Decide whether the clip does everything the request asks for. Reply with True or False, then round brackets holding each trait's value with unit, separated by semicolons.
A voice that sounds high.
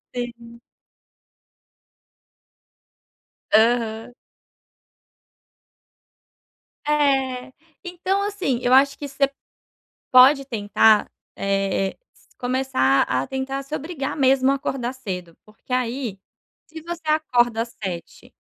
True (255 Hz)